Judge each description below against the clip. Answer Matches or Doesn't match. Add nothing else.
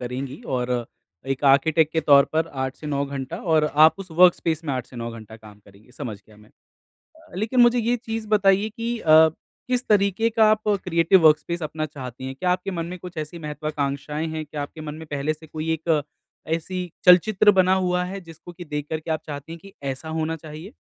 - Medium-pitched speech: Matches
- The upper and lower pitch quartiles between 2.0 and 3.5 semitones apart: Doesn't match